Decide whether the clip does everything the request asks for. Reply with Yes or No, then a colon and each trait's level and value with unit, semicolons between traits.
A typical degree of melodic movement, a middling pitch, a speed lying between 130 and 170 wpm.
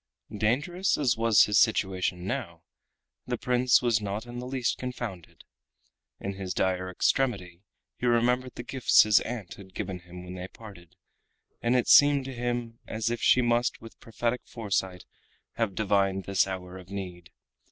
No: average, 4.5 semitones; low, 110 Hz; average, 165 wpm